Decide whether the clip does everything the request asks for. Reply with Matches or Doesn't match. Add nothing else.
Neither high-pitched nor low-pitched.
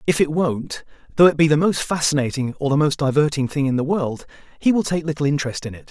Matches